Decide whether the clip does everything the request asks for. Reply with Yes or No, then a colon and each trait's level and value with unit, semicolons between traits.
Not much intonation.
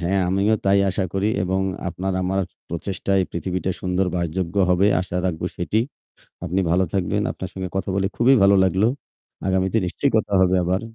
Yes: narrow, 1.4 semitones